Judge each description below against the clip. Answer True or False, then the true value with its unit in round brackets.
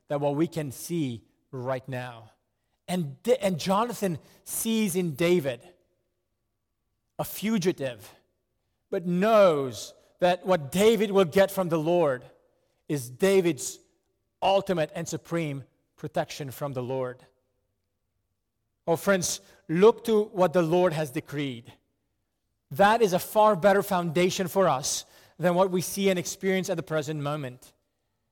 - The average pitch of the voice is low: False (160 Hz)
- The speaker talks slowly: True (130 wpm)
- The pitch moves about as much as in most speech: False (7.1 semitones)